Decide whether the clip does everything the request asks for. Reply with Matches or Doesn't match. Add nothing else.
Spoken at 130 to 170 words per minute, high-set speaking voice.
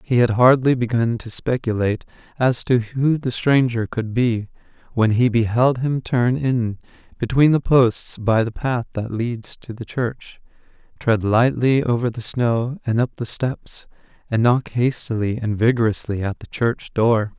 Doesn't match